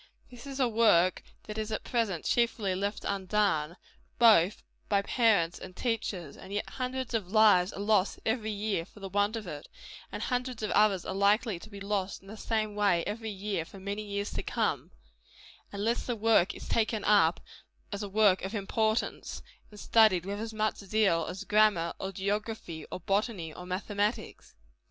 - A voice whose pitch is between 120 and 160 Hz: No, high, 205 Hz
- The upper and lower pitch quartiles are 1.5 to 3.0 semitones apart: Yes, narrow, 2.5 semitones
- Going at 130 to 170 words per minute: No, average, 180 wpm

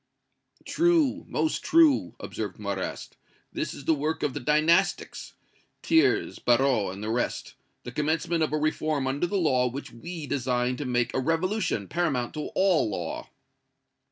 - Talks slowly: No, average, 155 wpm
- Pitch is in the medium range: Yes, medium, 150 Hz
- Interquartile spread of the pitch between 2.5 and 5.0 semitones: No, wide, 5.4 semitones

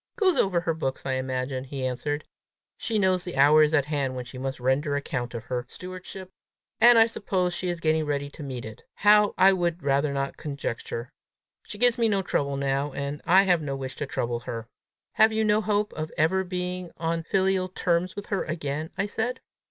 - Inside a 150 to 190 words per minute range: No, fast, 205 wpm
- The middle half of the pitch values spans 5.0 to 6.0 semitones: Yes, wide, 5.5 semitones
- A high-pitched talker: No, medium, 155 Hz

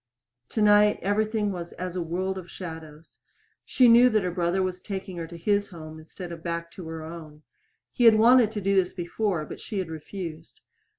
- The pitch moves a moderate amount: Yes, average, 3.7 semitones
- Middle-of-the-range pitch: Yes, medium, 180 Hz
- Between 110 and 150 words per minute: No, average, 195 wpm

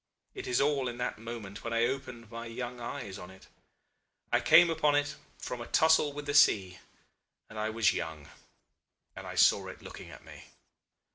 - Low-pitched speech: Yes, low, 120 Hz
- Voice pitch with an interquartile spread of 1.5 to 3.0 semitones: No, average, 4.7 semitones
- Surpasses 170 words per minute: Yes, average, 190 wpm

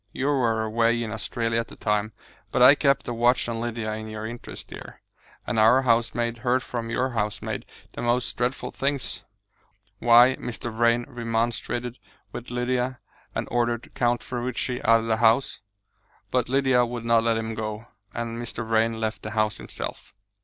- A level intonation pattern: Yes, narrow, 1.5 semitones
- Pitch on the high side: No, low, 120 Hz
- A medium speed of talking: Yes, average, 170 wpm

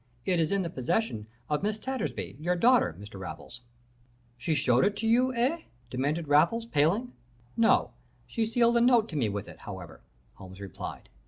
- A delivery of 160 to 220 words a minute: Yes, average, 175 wpm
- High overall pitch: No, medium, 175 Hz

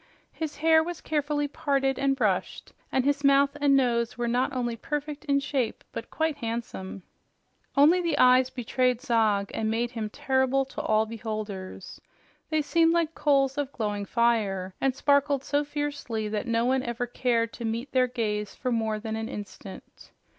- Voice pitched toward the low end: No, very high, 255 Hz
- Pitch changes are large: No, average, 4.1 semitones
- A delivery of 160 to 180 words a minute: Yes, average, 170 wpm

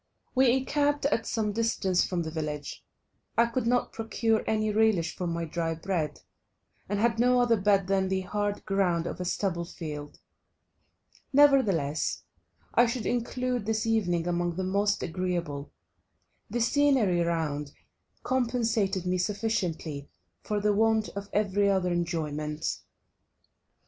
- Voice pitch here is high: Yes, high, 200 Hz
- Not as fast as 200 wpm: Yes, slow, 135 wpm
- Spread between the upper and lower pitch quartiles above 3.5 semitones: Yes, average, 4.7 semitones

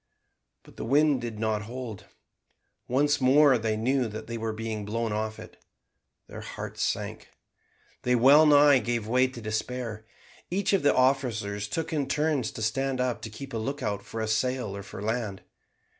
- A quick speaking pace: No, average, 175 wpm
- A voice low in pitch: Yes, low, 120 Hz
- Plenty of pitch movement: No, average, 3.7 semitones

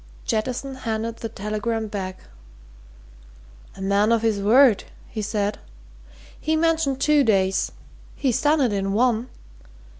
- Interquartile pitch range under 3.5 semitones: No, average, 4.2 semitones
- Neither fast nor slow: No, slow, 125 wpm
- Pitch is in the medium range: No, high, 225 Hz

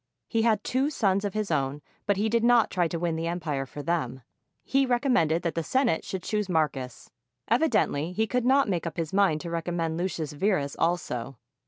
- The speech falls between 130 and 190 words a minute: No, average, 200 wpm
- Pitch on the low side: No, medium, 175 Hz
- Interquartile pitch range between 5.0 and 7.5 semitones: Yes, wide, 5.5 semitones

